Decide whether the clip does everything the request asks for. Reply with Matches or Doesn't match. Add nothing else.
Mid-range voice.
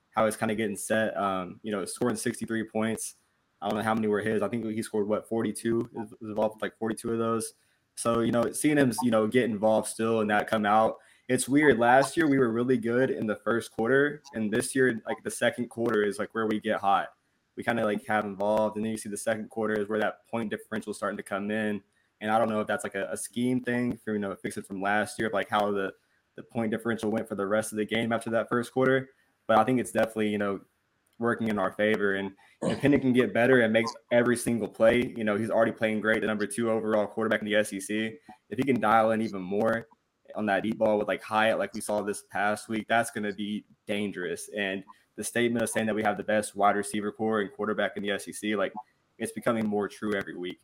Doesn't match